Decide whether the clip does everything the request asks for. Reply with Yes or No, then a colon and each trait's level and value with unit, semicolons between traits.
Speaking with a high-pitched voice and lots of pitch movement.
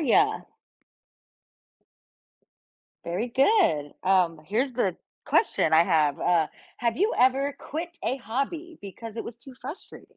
Yes: high, 240 Hz; wide, 7.9 semitones